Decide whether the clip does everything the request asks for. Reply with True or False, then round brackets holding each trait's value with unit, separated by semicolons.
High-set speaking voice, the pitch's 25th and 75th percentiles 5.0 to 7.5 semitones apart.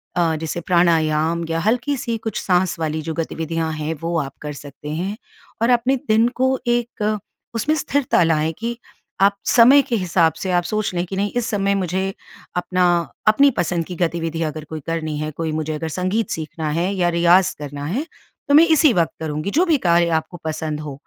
False (175 Hz; 5.3 semitones)